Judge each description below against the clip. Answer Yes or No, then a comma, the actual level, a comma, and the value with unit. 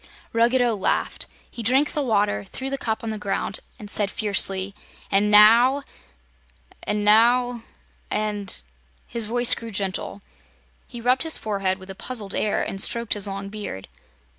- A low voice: No, high, 210 Hz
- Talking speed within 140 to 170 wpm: Yes, average, 160 wpm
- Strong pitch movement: No, average, 3.2 semitones